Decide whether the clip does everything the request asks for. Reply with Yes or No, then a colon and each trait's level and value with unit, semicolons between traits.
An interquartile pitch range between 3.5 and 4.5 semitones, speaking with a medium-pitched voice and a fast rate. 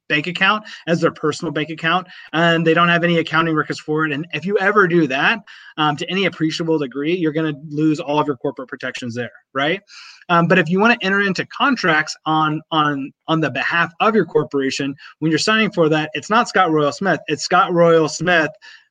No: average, 3.1 semitones; medium, 160 Hz; fast, 220 wpm